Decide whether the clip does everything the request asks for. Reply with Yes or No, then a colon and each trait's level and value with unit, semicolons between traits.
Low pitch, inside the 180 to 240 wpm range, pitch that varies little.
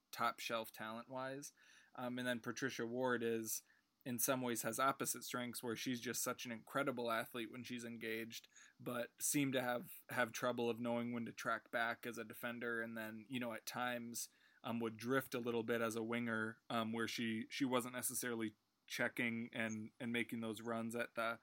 Yes: low, 120 Hz; average, 195 wpm; narrow, 1.5 semitones